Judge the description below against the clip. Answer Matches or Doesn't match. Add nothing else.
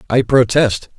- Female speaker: Doesn't match